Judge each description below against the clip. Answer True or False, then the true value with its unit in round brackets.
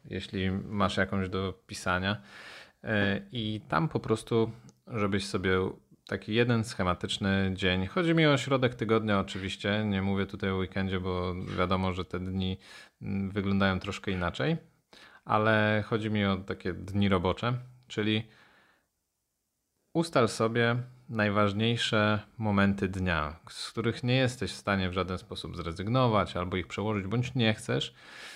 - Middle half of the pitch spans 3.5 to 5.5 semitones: False (3.1 semitones)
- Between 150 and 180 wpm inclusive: False (135 wpm)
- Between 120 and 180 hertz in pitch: False (100 Hz)